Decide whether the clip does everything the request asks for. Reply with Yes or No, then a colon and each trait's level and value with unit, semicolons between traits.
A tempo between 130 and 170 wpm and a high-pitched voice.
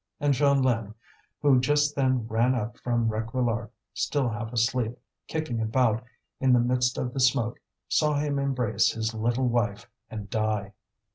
No: average, 150 wpm; low, 120 Hz